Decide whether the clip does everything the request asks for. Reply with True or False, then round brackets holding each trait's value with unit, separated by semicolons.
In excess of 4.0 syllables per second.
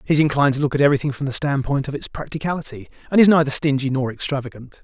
True (7.6 syllables/s)